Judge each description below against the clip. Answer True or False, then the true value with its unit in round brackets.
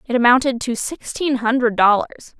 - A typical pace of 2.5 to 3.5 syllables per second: False (5.6 syllables/s)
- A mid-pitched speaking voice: False (240 Hz)